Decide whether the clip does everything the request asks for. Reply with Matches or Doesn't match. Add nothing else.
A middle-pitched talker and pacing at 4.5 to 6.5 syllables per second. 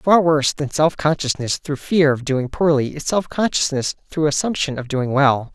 Matches